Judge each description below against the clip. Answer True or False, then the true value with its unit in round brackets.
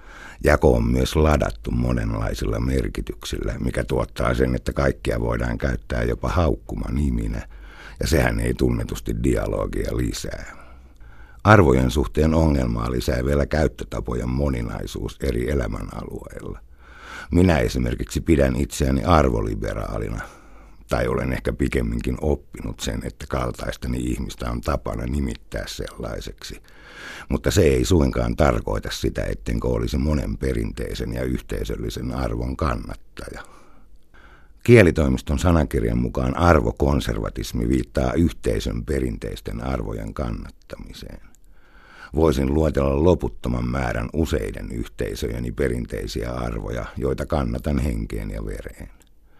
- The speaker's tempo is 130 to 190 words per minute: False (105 wpm)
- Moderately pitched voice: False (65 Hz)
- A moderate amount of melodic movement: True (3.2 semitones)